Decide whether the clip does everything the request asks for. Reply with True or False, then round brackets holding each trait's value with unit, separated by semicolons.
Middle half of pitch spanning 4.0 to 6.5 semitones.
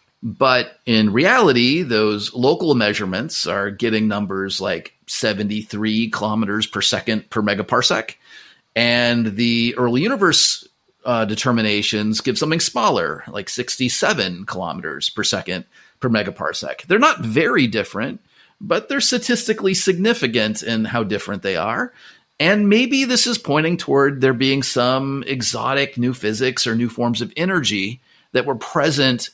True (4.4 semitones)